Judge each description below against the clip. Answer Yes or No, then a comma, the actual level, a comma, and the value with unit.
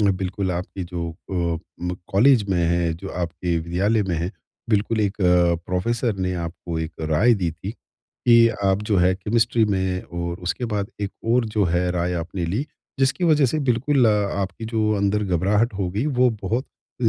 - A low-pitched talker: Yes, very low, 95 Hz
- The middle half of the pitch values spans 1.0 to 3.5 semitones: No, average, 4.0 semitones